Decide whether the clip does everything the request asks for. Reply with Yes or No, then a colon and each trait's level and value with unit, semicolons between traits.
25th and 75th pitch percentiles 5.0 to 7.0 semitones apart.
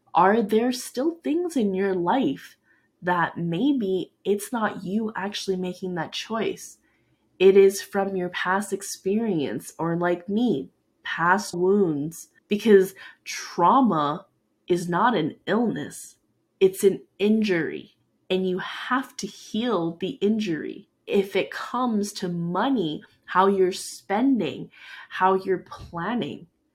No: average, 3.3 semitones